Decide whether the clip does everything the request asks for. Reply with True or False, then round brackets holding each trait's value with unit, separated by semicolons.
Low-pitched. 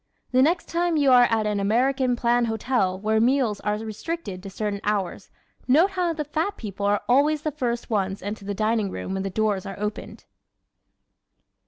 False (225 Hz)